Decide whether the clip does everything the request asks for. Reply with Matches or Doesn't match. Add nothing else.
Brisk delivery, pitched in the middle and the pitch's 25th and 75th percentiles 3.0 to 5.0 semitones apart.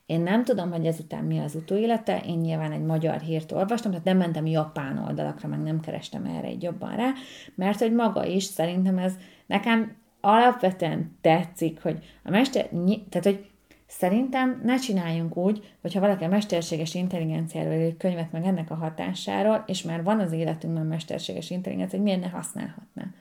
Matches